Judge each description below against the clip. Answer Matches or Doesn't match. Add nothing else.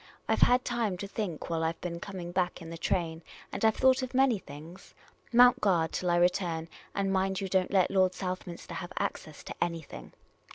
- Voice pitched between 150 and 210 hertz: Matches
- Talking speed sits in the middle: Doesn't match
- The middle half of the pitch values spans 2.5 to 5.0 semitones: Matches